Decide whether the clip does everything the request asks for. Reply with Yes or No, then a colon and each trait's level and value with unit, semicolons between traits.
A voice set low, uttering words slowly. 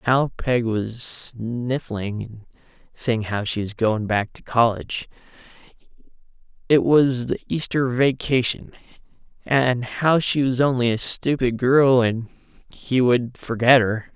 Yes: low, 120 Hz; slow, 125 wpm